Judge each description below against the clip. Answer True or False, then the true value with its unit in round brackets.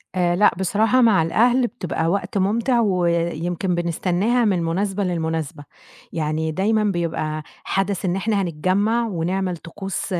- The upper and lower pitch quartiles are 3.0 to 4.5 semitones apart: True (3.6 semitones)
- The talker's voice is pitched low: False (185 Hz)